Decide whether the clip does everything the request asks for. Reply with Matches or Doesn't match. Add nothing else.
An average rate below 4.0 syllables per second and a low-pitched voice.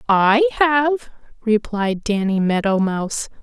Doesn't match